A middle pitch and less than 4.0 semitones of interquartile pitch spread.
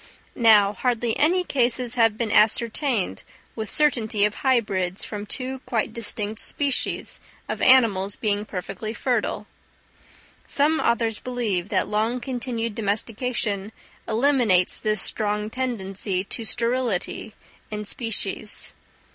No: high, 225 Hz; average, 3.1 semitones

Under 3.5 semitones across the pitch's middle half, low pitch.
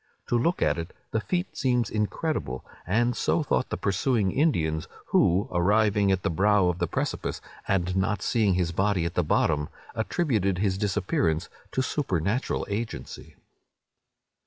No: average, 4.7 semitones; low, 100 Hz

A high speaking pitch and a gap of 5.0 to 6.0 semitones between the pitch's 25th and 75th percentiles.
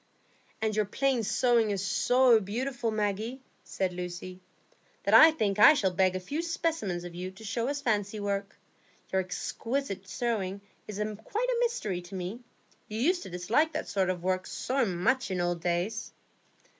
Yes: high, 210 Hz; wide, 5.4 semitones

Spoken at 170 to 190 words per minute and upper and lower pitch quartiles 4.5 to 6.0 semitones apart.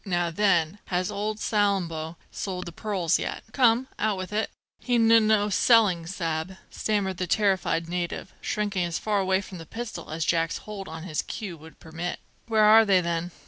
No: average, 185 wpm; average, 3.8 semitones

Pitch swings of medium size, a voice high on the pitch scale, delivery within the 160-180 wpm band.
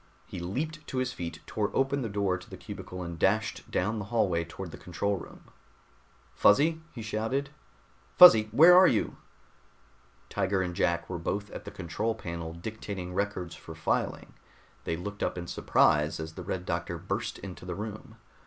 No: average, 4.2 semitones; low, 100 Hz; average, 175 wpm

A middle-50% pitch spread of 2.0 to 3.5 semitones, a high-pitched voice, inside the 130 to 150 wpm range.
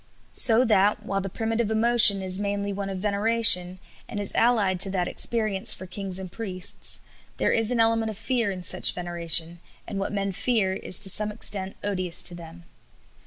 No: average, 3.1 semitones; high, 200 Hz; average, 185 wpm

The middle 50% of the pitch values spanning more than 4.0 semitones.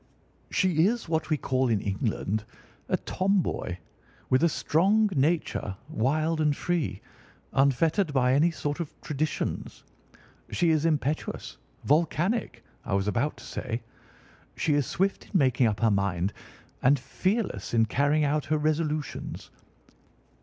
Yes: average, 4.8 semitones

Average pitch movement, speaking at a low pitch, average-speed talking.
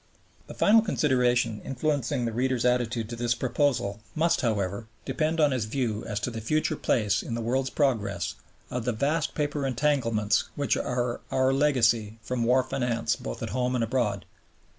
Yes: average, 3.3 semitones; low, 125 Hz; average, 170 wpm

